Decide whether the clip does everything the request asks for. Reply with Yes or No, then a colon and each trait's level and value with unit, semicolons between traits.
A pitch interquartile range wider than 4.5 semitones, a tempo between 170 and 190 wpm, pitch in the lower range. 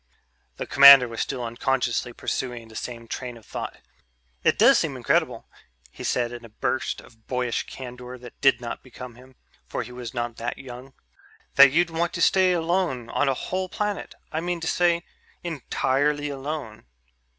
No: average, 4.1 semitones; average, 175 wpm; low, 130 Hz